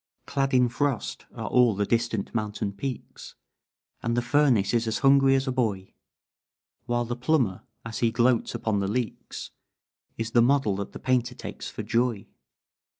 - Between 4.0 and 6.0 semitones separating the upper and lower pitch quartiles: No, average, 2.8 semitones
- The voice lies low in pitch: Yes, low, 120 Hz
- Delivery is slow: No, average, 165 wpm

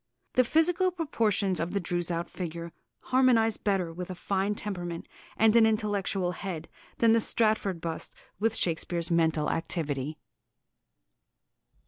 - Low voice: No, high, 190 Hz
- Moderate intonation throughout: Yes, average, 4.7 semitones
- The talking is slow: Yes, slow, 125 wpm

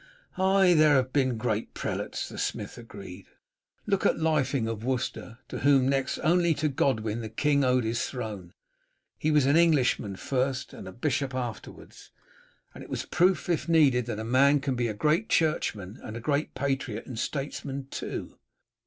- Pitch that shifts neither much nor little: Yes, average, 4.7 semitones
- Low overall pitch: Yes, low, 130 Hz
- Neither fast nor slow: Yes, average, 175 wpm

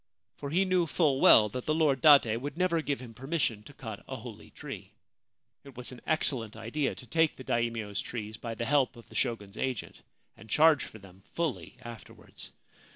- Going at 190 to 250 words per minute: Yes, average, 195 wpm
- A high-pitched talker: No, low, 130 Hz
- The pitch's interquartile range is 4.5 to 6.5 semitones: Yes, average, 4.9 semitones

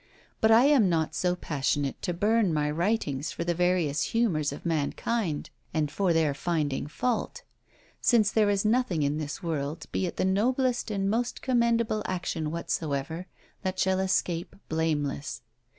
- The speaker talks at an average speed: Yes, average, 155 wpm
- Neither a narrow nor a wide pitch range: No, wide, 5.8 semitones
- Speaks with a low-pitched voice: No, medium, 175 Hz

